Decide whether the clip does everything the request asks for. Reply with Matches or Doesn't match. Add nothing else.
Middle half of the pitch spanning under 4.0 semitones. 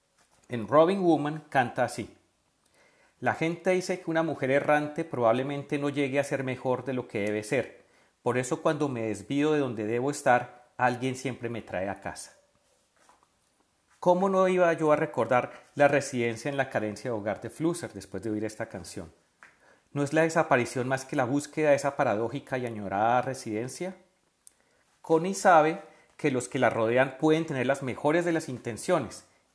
Doesn't match